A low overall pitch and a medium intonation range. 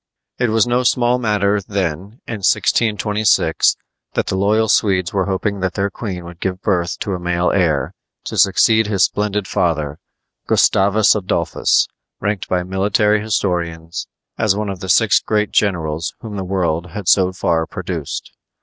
Yes: very low, 95 Hz; average, 3.0 semitones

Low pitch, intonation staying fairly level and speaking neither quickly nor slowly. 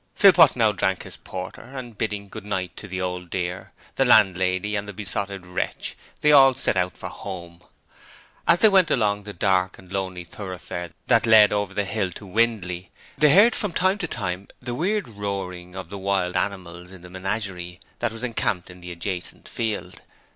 No: low, 100 Hz; average, 3.7 semitones; average, 190 wpm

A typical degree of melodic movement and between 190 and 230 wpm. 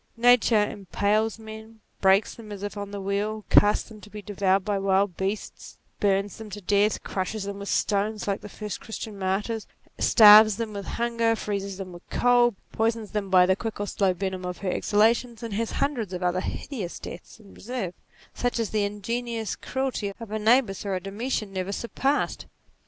No: narrow, 2.3 semitones; average, 195 wpm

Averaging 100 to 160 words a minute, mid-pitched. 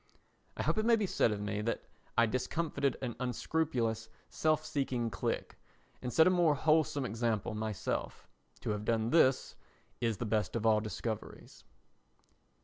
No: average, 155 wpm; low, 120 Hz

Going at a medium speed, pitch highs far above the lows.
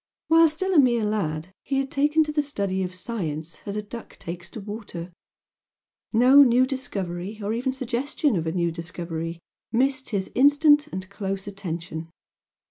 Yes: average, 165 wpm; wide, 7.3 semitones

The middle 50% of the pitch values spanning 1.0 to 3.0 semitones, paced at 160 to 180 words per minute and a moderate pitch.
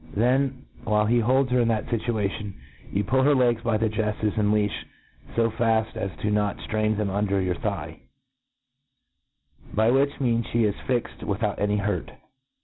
No: narrow, 2.4 semitones; average, 175 wpm; low, 110 Hz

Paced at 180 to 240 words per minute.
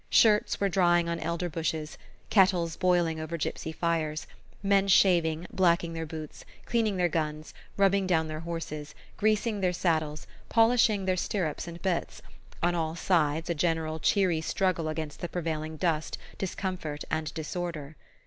No: average, 150 wpm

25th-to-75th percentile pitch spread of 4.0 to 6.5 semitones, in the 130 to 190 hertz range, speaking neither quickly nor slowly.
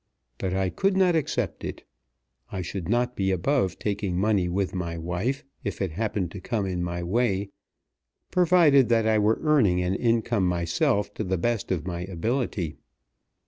No: average, 5.0 semitones; low, 100 Hz; average, 170 wpm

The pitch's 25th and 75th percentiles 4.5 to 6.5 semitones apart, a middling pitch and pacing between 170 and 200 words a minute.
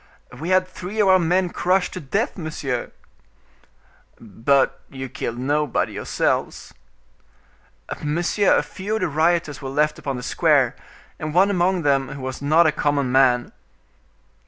No: average, 5.0 semitones; medium, 150 Hz; average, 150 wpm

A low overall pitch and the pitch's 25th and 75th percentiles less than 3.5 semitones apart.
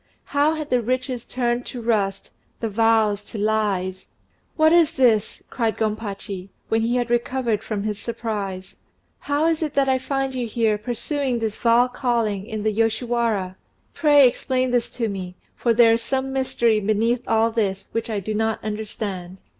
No: high, 230 Hz; average, 2.9 semitones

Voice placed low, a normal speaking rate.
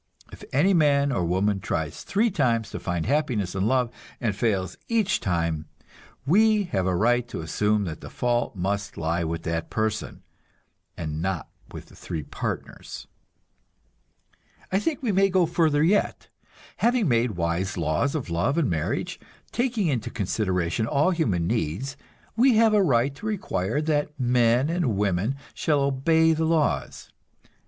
Yes: low, 120 Hz; average, 155 wpm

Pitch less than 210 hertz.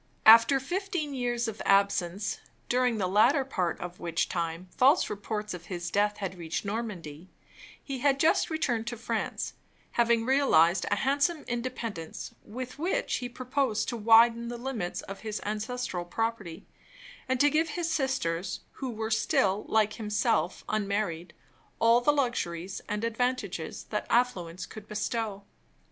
No: high, 225 Hz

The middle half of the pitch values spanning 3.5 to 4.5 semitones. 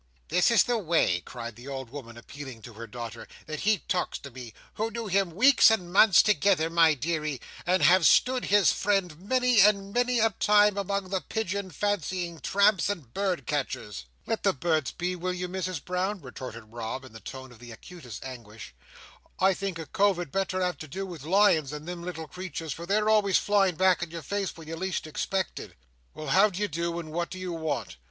No: average, 5.3 semitones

